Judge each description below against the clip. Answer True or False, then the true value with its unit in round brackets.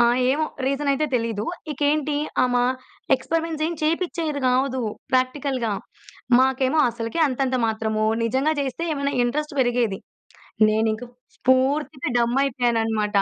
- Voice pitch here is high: True (260 Hz)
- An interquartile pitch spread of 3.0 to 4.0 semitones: True (3.7 semitones)